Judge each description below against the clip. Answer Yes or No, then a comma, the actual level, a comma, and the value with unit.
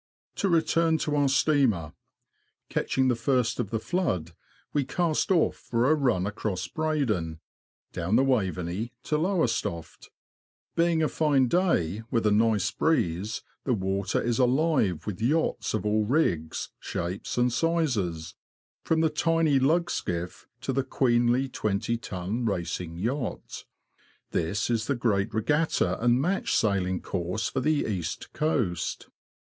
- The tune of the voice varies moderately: No, wide, 7.6 semitones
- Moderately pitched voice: No, low, 120 Hz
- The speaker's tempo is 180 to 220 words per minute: No, average, 140 wpm